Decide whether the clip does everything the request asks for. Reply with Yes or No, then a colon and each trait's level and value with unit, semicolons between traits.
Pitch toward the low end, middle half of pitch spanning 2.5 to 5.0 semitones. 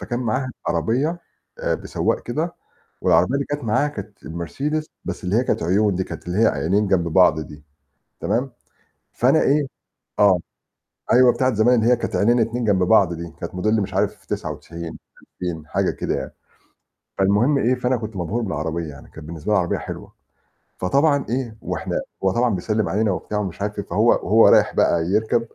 No: low, 105 Hz; wide, 5.5 semitones